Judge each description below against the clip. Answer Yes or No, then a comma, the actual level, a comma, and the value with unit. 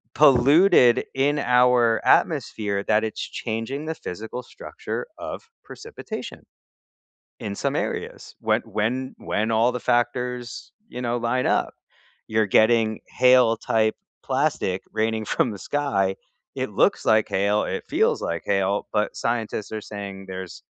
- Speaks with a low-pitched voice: Yes, low, 115 Hz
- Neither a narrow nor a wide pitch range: Yes, average, 3.0 semitones